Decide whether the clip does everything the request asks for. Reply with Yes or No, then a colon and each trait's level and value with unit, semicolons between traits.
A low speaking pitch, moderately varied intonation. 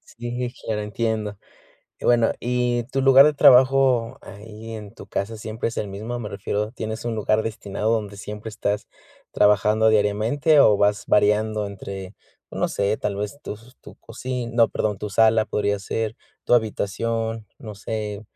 No: low, 110 Hz; narrow, 2.1 semitones